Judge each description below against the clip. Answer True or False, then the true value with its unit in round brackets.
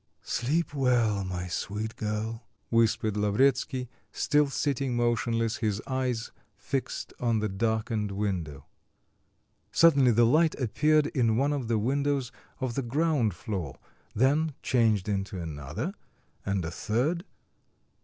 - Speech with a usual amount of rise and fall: True (4.4 semitones)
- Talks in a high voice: False (115 Hz)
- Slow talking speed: True (125 wpm)